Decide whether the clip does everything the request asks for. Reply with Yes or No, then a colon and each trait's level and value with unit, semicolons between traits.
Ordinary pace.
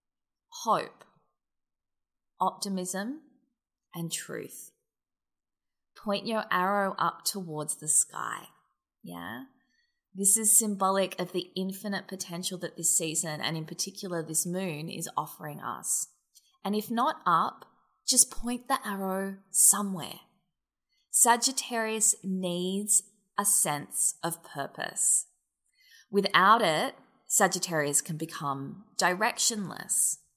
No: slow, 100 wpm